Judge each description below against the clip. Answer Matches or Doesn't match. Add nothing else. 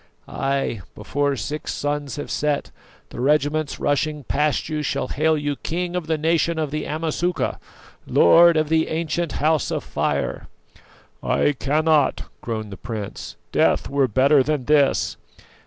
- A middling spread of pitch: Doesn't match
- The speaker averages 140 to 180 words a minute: Matches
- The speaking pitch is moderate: Matches